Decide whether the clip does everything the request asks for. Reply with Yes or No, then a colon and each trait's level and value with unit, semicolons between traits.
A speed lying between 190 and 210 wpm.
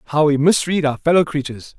Yes: average, 200 wpm